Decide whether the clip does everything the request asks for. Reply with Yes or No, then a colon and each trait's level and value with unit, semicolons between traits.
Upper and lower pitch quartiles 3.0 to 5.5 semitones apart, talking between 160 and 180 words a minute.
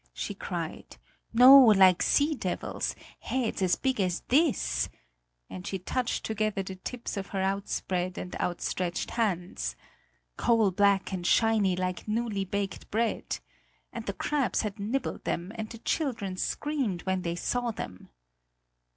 No: average, 4.0 semitones; average, 140 wpm